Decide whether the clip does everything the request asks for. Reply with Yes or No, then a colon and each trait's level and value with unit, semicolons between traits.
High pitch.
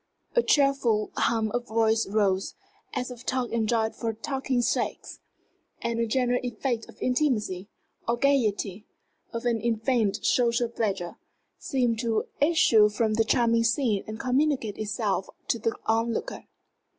Yes: high, 230 Hz